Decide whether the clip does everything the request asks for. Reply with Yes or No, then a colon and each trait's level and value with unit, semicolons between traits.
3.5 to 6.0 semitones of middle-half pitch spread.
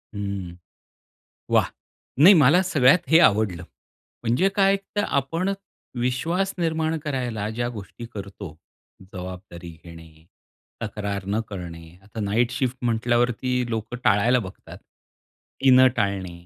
Yes: average, 5.0 semitones